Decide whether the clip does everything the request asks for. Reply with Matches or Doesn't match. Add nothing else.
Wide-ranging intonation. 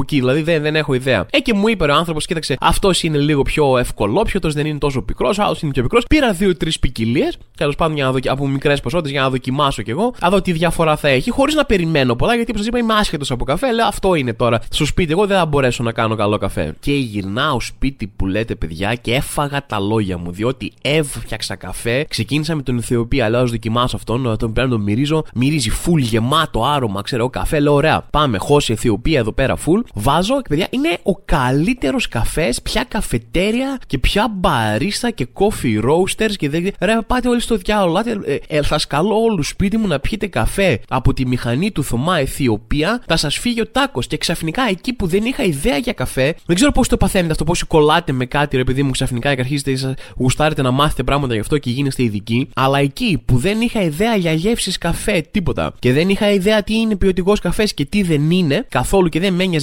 Matches